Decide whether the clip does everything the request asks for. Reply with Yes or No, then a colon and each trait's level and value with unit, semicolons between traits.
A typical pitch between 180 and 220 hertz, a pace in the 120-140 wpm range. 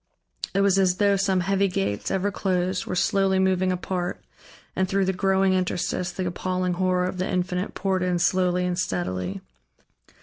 No: medium, 185 Hz; average, 170 wpm